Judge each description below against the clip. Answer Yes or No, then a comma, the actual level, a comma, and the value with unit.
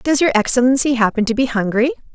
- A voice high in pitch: Yes, high, 245 Hz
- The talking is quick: No, average, 195 wpm